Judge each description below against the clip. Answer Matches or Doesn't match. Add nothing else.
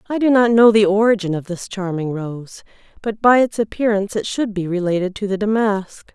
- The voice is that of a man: Doesn't match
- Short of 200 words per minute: Doesn't match